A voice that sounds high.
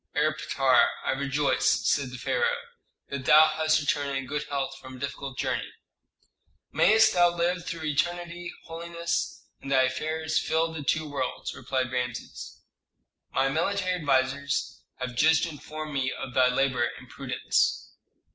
No: medium, 145 Hz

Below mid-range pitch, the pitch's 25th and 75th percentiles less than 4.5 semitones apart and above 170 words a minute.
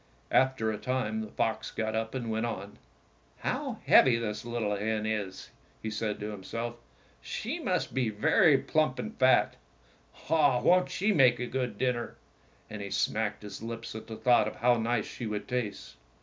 Yes: low, 115 Hz; average, 2.7 semitones; average, 180 wpm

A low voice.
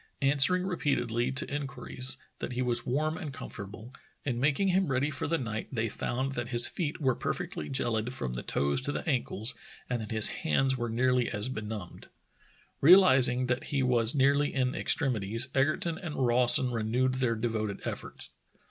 Yes: low, 125 Hz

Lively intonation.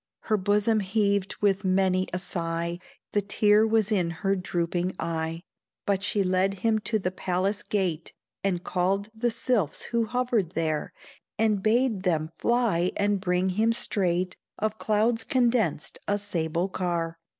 No: average, 3.3 semitones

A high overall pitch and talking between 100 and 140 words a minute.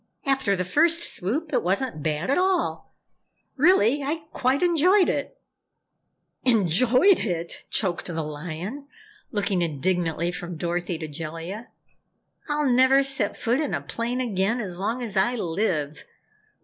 Yes: high, 210 Hz; slow, 135 wpm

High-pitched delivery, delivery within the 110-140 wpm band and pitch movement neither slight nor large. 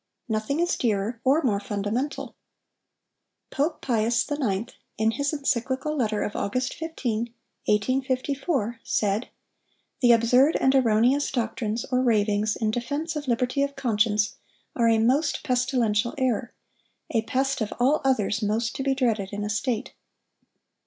Yes: high, 240 Hz; slow, 135 wpm; average, 3.8 semitones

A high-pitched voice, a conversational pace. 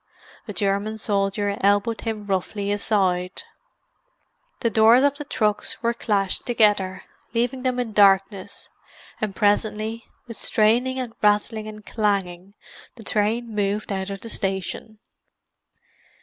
No: high, 210 Hz; slow, 125 wpm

